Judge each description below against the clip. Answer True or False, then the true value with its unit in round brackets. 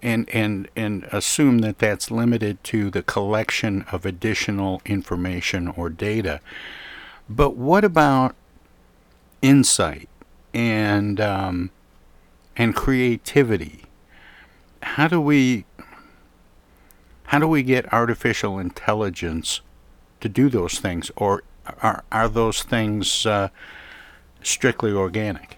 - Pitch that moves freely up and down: False (4.8 semitones)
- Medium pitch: False (105 Hz)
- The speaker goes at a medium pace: False (105 wpm)